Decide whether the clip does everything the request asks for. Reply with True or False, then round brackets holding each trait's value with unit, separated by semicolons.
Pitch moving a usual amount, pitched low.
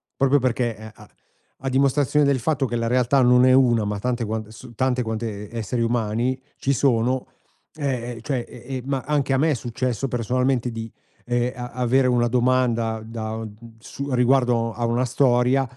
False (2.2 semitones; 125 Hz)